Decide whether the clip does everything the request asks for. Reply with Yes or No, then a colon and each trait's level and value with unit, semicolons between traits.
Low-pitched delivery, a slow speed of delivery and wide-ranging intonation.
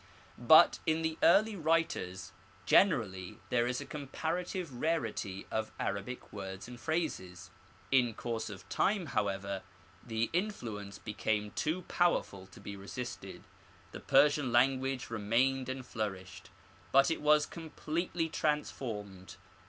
Yes: low, 125 Hz; slow, 130 wpm; wide, 7.6 semitones